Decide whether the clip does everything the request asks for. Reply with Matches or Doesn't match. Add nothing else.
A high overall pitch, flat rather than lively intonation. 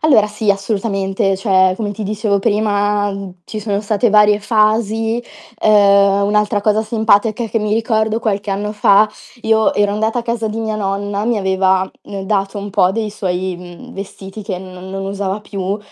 Matches